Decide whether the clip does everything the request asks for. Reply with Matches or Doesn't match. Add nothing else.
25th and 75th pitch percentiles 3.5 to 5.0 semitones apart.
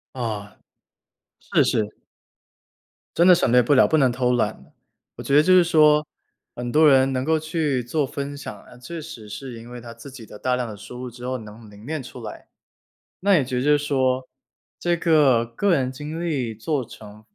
Matches